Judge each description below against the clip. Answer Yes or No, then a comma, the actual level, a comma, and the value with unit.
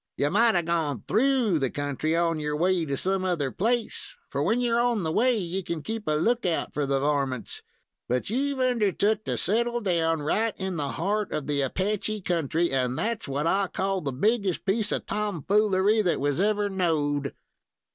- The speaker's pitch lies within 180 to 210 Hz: Yes, medium, 185 Hz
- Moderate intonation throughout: No, wide, 6.1 semitones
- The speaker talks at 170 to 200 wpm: Yes, average, 190 wpm